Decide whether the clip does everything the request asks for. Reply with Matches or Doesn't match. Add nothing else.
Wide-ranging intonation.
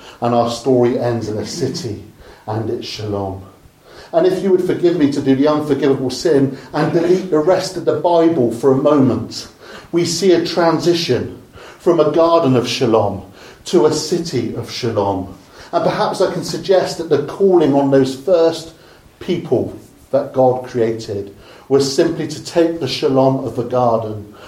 Matches